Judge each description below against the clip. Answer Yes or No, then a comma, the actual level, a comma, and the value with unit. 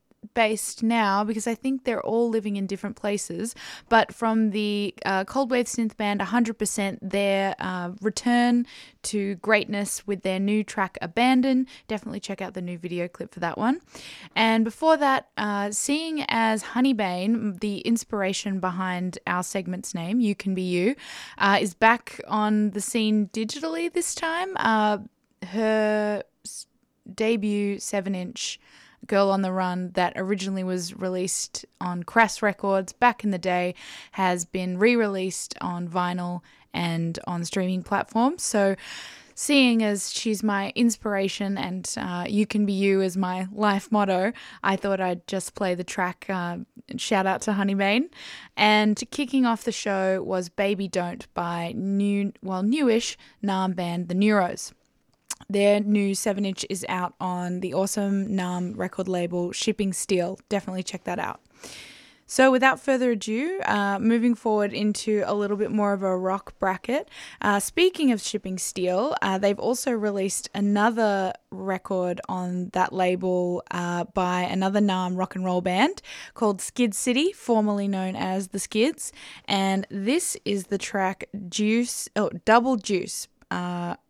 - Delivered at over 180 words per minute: No, average, 155 wpm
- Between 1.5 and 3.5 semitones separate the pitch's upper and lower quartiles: Yes, average, 3.1 semitones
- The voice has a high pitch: Yes, high, 200 Hz